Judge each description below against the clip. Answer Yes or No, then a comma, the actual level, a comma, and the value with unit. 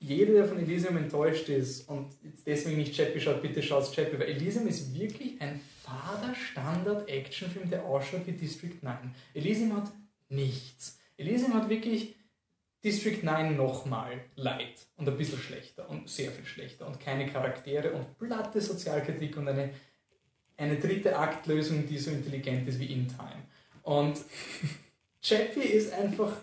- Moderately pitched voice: Yes, medium, 150 Hz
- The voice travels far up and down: Yes, wide, 6.4 semitones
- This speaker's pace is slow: No, average, 150 wpm